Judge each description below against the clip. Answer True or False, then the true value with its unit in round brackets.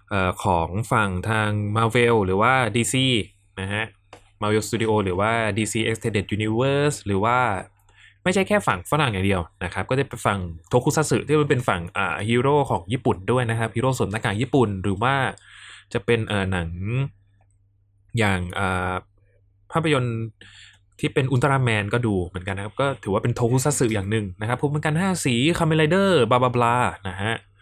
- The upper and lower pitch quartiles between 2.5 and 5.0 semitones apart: True (4.7 semitones)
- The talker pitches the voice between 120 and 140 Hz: False (110 Hz)